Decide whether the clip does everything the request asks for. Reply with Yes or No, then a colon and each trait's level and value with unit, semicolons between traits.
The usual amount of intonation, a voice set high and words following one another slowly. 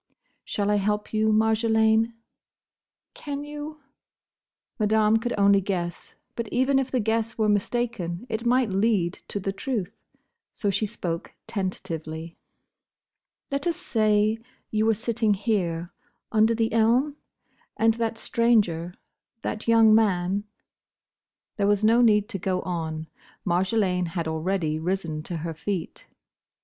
Yes: average, 3.7 semitones; high, 210 Hz; slow, 130 wpm